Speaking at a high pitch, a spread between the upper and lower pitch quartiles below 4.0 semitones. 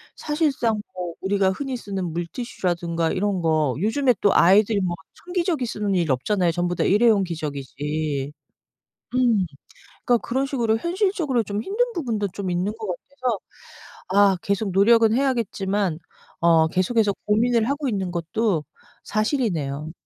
No: high, 205 Hz; wide, 5.5 semitones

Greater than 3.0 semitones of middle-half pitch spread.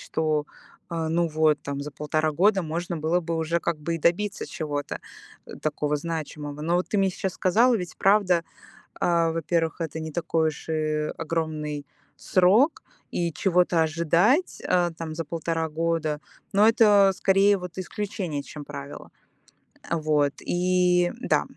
No: average, 2.7 semitones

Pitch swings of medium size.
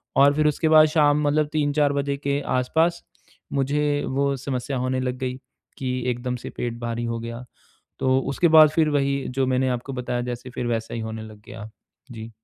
Yes: average, 3.0 semitones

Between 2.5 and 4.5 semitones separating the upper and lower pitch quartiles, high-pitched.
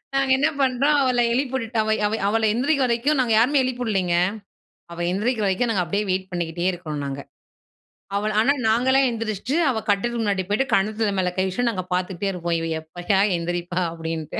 No: average, 5.3 semitones; high, 215 Hz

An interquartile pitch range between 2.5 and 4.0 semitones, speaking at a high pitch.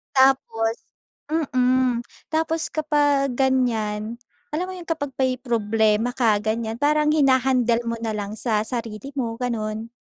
Yes: average, 3.6 semitones; very high, 250 Hz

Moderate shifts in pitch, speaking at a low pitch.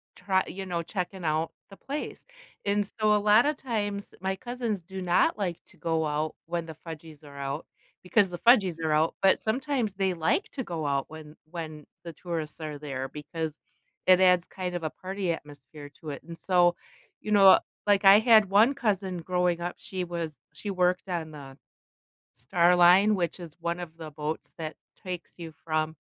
No: average, 3.7 semitones; medium, 175 Hz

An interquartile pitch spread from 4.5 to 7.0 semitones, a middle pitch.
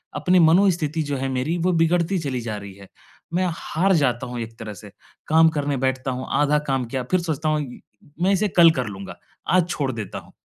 Yes: average, 5.1 semitones; medium, 145 Hz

